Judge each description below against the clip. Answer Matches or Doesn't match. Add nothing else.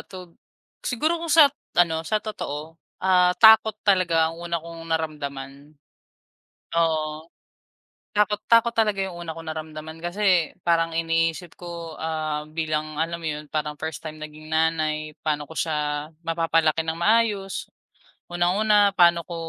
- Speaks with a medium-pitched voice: Matches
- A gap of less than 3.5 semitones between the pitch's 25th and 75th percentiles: Matches